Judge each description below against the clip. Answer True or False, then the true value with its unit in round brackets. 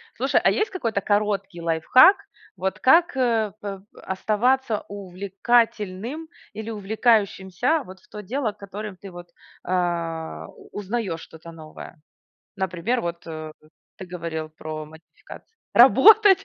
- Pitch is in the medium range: False (200 Hz)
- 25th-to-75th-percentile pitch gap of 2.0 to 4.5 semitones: False (5.1 semitones)